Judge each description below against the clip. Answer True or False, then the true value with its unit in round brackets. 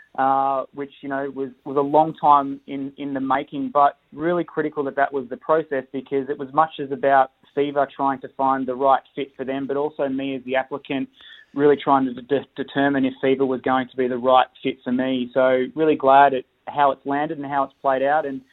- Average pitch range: False (1.1 semitones)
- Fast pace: True (230 wpm)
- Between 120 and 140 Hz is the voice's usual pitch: True (135 Hz)